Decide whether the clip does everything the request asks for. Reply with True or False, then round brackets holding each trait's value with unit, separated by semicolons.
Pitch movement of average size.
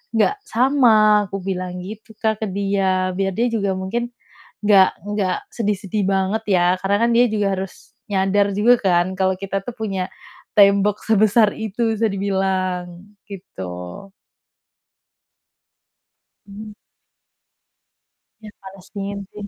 False (2.2 semitones)